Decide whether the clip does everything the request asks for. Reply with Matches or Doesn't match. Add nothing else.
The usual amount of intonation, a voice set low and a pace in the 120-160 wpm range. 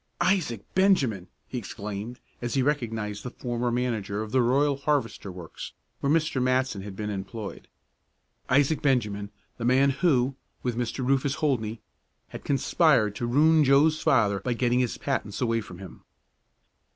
Matches